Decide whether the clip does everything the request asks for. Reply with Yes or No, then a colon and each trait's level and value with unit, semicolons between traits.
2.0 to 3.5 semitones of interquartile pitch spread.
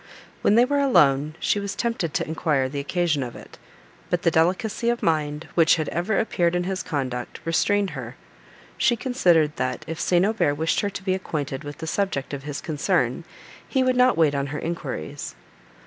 No: wide, 5.4 semitones